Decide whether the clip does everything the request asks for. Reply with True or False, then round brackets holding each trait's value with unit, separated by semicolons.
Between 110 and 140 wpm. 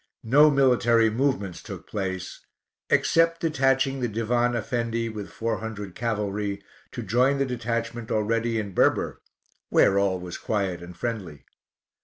True (135 wpm)